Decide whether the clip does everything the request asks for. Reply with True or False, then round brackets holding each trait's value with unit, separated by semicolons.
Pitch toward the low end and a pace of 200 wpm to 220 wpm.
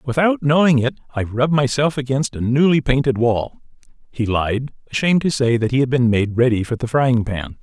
True (130 Hz; 205 wpm)